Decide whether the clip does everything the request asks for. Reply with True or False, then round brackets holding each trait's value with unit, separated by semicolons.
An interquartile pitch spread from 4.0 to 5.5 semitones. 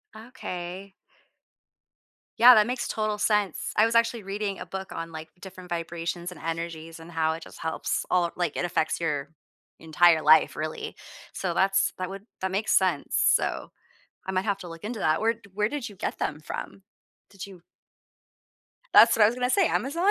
True (4.3 semitones)